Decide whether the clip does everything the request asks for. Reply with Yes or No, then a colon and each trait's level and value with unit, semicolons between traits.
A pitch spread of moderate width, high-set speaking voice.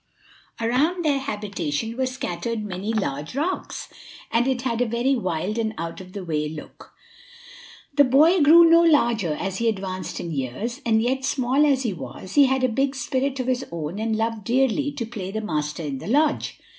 No: wide, 6.2 semitones; high, 230 Hz